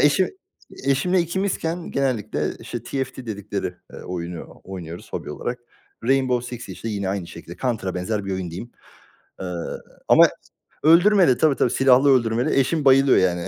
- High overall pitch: No, low, 120 Hz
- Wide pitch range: Yes, wide, 6.4 semitones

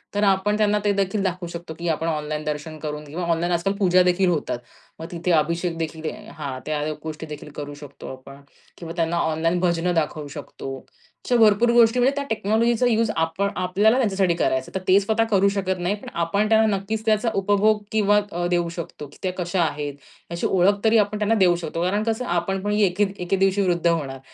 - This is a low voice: No, medium, 180 Hz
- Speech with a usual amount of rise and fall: Yes, average, 4.0 semitones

